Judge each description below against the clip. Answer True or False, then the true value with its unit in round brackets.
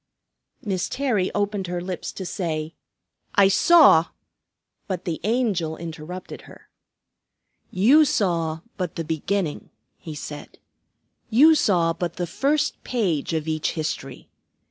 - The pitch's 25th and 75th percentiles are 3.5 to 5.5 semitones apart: True (4.2 semitones)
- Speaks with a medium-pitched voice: True (180 Hz)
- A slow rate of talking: True (125 wpm)